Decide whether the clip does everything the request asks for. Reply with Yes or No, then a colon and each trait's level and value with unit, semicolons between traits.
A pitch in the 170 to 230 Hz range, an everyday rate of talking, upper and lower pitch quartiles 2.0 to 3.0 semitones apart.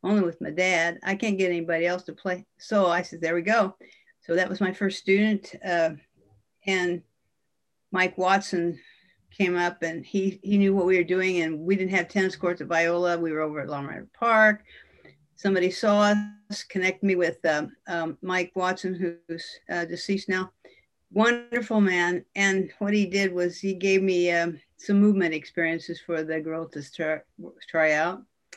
Yes: medium, 185 Hz; average, 180 wpm; narrow, 2.6 semitones